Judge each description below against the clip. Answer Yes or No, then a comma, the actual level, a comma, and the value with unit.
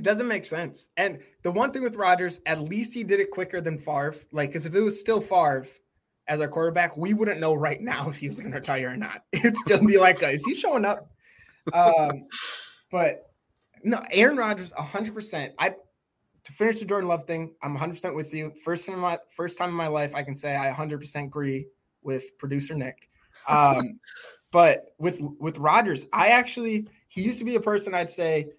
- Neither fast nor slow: No, fast, 210 wpm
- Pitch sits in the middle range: Yes, medium, 175 Hz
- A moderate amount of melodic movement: No, wide, 5.8 semitones